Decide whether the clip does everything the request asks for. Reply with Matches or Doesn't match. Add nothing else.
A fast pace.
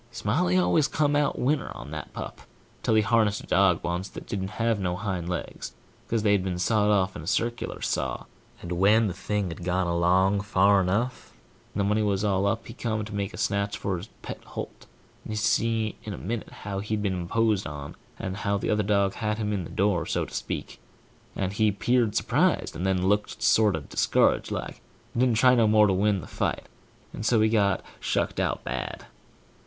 Matches